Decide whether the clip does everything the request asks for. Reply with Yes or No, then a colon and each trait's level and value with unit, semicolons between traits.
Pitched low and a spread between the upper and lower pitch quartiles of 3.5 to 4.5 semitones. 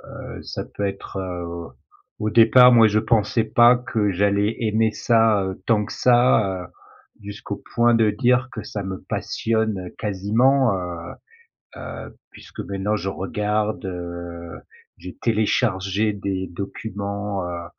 No: low, 105 Hz; average, 2.9 semitones